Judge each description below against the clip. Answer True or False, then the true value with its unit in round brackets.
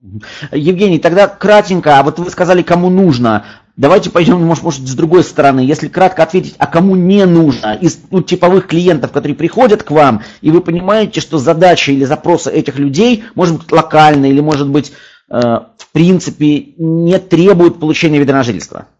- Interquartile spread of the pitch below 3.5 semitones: False (3.8 semitones)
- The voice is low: False (165 Hz)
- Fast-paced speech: True (170 wpm)